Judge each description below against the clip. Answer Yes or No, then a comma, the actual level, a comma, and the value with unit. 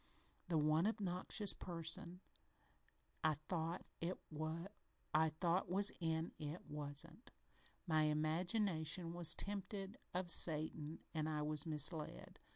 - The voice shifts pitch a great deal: No, average, 2.8 semitones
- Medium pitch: Yes, medium, 165 Hz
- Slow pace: Yes, slow, 95 wpm